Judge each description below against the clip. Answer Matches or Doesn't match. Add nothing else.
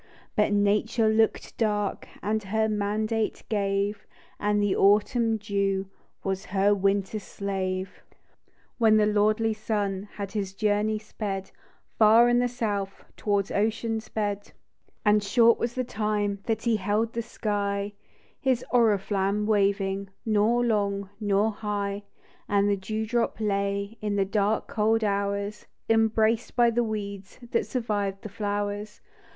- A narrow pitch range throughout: Matches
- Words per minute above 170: Doesn't match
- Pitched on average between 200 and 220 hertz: Matches